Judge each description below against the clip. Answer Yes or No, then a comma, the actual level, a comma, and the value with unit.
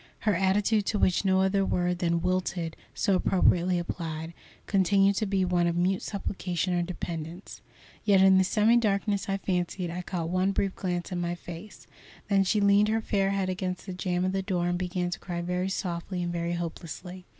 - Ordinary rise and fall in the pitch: No, narrow, 1.9 semitones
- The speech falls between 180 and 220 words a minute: Yes, average, 195 wpm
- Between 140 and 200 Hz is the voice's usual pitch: Yes, medium, 185 Hz